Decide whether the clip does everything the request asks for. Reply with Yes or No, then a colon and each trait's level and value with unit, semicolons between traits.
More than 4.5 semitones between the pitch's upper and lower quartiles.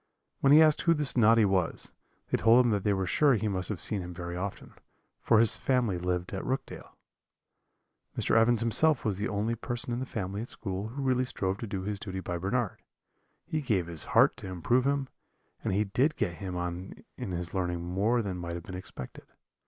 Yes: average, 4.9 semitones